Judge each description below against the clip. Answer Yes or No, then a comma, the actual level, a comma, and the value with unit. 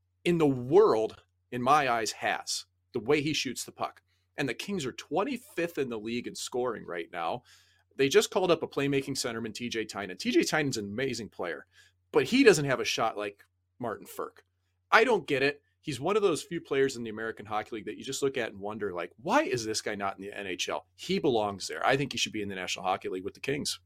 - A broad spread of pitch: Yes, wide, 6.2 semitones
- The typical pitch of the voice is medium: No, low, 120 Hz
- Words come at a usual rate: No, fast, 240 wpm